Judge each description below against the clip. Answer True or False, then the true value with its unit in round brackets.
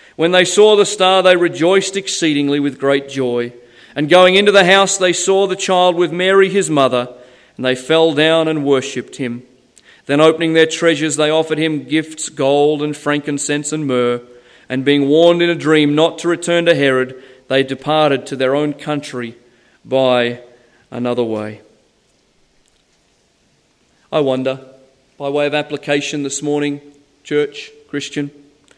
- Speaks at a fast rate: False (155 wpm)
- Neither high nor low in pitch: True (145 Hz)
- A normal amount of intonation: True (4.1 semitones)